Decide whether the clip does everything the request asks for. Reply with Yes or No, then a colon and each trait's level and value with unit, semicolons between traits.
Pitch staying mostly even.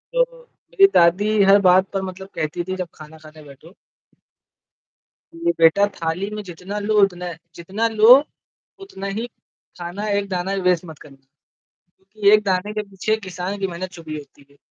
No: average, 3.1 semitones